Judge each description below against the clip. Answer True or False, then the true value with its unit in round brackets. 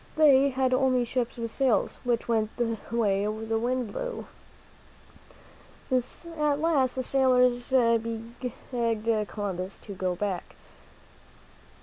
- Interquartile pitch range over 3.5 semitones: False (2.8 semitones)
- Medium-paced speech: False (110 wpm)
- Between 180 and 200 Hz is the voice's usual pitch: False (240 Hz)